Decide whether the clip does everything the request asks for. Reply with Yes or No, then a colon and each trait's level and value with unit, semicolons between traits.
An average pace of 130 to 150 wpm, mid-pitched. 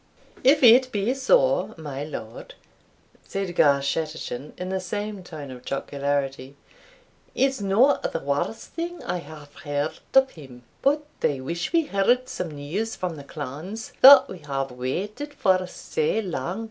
Yes: average, 145 wpm; medium, 180 Hz